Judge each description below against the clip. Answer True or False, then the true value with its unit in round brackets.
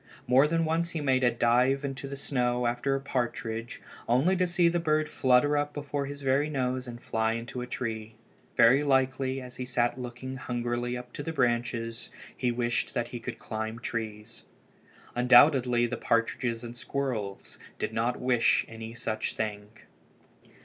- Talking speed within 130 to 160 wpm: False (170 wpm)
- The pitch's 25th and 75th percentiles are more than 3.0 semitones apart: False (2.6 semitones)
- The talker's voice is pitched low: True (125 Hz)